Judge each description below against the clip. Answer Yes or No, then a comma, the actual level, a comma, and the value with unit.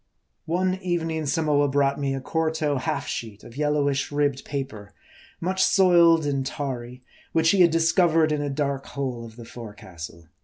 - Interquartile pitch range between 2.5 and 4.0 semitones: Yes, average, 3.5 semitones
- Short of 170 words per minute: Yes, average, 160 wpm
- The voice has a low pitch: No, medium, 145 Hz